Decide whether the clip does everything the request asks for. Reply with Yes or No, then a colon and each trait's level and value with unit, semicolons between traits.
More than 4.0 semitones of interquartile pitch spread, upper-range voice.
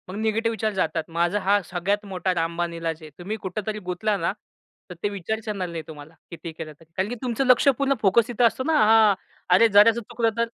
Yes: average, 4.5 semitones; high, 200 Hz